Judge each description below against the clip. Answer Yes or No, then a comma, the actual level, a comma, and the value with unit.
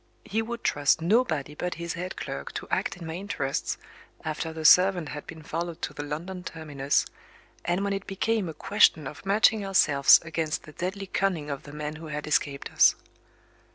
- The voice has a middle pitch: Yes, medium, 165 Hz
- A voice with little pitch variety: No, average, 4.4 semitones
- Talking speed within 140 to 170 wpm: No, average, 190 wpm